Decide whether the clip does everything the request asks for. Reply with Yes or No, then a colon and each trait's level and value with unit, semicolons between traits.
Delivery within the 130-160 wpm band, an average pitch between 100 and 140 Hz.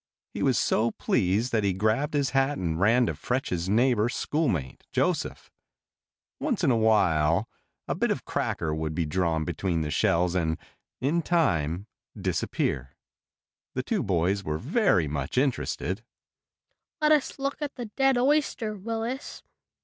Yes: average, 150 wpm; low, 110 Hz